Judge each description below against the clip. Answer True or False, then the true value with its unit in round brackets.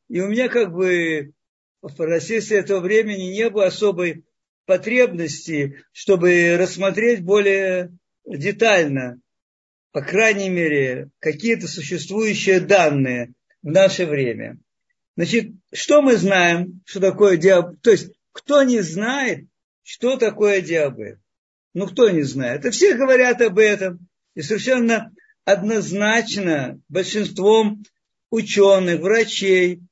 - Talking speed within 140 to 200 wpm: False (115 wpm)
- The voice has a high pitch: True (195 Hz)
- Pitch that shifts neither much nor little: True (4.4 semitones)